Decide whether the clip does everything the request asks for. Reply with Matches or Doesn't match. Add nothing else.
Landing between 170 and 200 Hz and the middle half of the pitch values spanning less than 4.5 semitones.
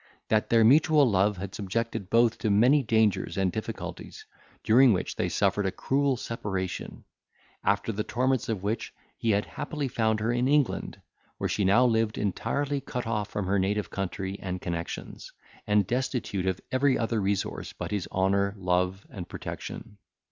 Doesn't match